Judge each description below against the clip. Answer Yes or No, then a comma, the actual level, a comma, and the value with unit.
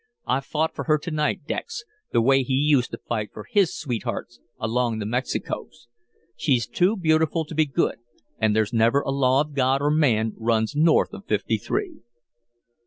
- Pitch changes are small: No, average, 4.6 semitones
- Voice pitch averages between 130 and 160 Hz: Yes, low, 135 Hz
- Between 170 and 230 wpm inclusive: Yes, average, 180 wpm